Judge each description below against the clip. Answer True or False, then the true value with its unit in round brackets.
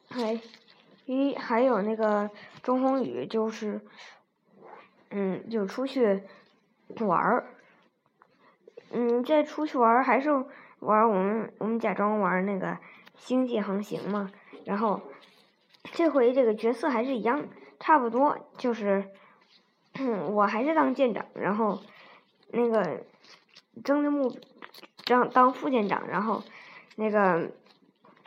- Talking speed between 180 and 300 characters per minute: False (170 characters per minute)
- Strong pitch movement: False (4.1 semitones)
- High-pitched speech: True (230 Hz)